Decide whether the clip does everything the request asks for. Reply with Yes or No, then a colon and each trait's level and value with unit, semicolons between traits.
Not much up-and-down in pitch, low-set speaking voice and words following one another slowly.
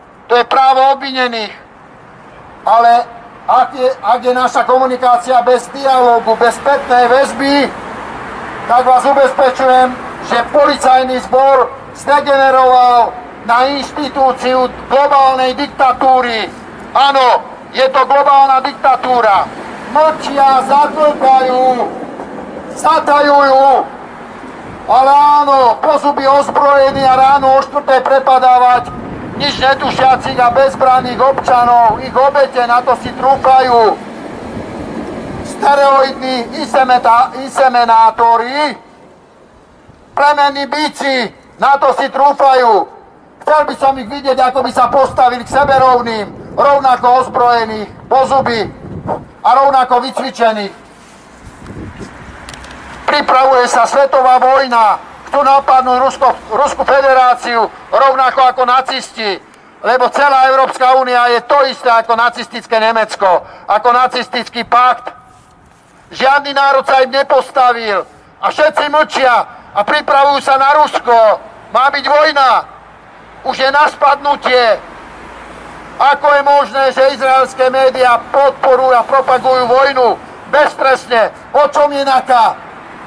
No: narrow, 2.1 semitones; very high, 265 Hz; slow, 100 wpm